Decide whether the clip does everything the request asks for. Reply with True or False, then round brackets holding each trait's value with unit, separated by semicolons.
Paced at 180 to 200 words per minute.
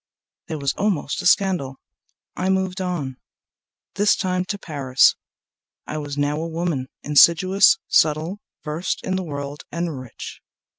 False (145 wpm)